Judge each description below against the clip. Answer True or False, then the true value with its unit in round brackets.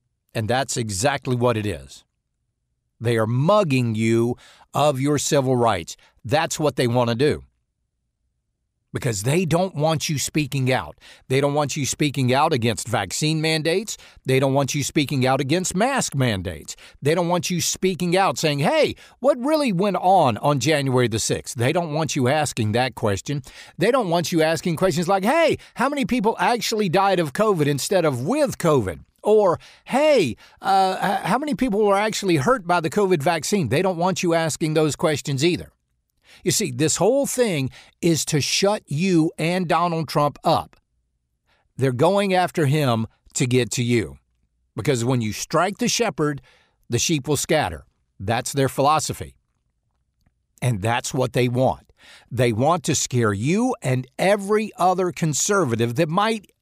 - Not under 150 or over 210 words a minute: True (165 wpm)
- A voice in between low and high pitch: True (150 Hz)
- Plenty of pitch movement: True (6.6 semitones)